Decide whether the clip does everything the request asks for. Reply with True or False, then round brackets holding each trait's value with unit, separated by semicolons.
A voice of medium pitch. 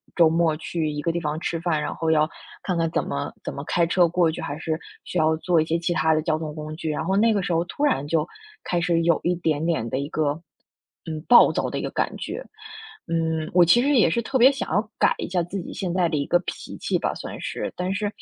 True (165 Hz)